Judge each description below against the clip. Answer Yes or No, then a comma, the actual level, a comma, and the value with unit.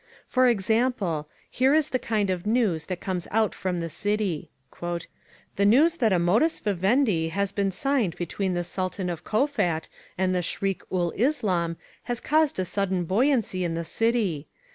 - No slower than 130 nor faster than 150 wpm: No, average, 165 wpm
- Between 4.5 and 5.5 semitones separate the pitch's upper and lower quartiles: Yes, average, 5.1 semitones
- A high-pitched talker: Yes, high, 195 Hz